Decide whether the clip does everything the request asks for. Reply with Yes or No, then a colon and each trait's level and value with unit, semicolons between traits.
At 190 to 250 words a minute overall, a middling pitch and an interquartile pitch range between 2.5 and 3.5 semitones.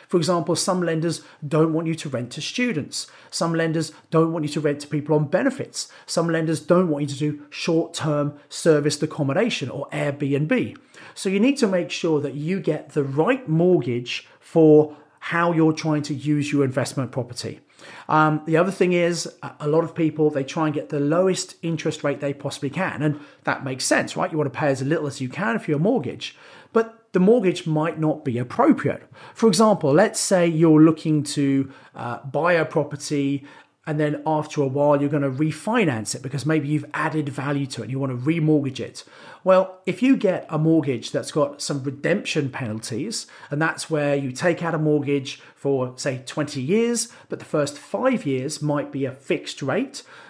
Yes: average, 200 wpm; medium, 155 Hz; average, 2.8 semitones